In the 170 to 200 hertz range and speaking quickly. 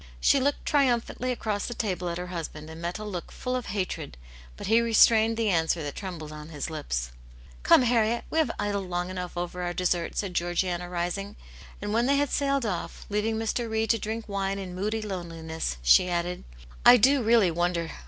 Yes: high, 190 Hz; fast, 210 wpm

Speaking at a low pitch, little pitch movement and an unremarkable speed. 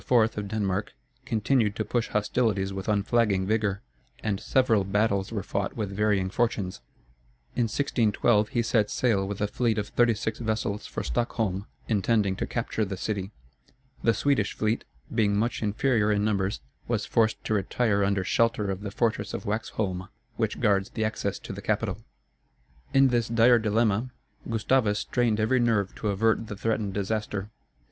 Yes: low, 105 Hz; narrow, 2.3 semitones; average, 160 wpm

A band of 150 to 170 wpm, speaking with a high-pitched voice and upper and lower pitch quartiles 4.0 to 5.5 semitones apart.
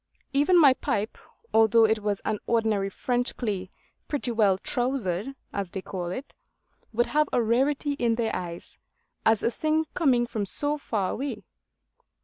Yes: average, 155 wpm; high, 230 Hz; average, 5.0 semitones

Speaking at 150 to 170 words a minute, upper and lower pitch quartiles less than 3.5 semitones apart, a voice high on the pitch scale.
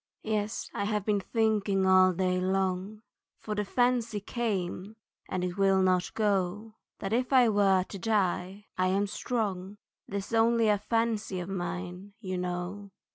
Yes: average, 155 wpm; narrow, 2.6 semitones; high, 200 Hz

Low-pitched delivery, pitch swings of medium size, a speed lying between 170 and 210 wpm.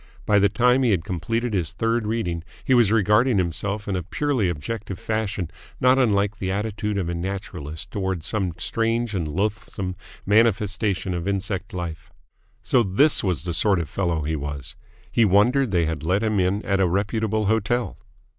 Yes: low, 100 Hz; average, 3.7 semitones; average, 175 wpm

